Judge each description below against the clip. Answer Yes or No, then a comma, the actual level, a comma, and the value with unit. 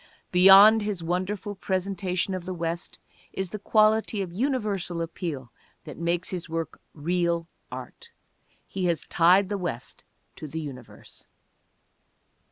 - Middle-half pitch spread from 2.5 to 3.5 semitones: Yes, average, 2.9 semitones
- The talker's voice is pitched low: No, medium, 180 Hz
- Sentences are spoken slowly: Yes, slow, 130 wpm